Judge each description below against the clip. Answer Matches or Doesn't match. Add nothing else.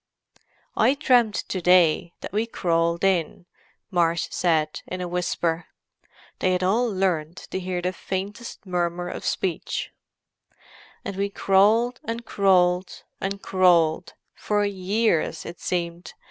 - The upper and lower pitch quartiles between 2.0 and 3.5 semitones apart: Matches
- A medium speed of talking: Doesn't match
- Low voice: Doesn't match